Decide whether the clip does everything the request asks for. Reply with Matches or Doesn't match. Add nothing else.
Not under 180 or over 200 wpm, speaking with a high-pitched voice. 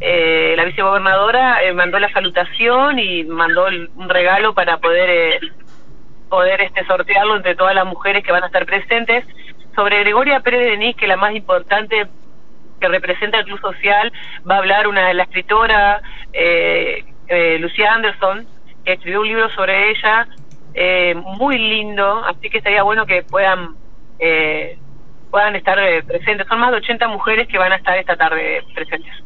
Doesn't match